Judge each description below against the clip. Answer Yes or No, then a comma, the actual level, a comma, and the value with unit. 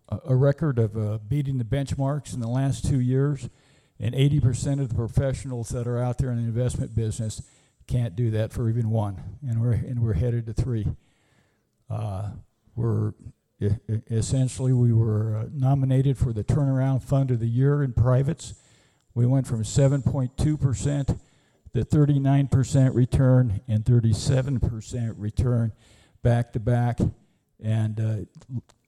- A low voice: Yes, low, 120 Hz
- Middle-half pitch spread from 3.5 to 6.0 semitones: No, average, 3.1 semitones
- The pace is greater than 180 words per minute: No, average, 150 wpm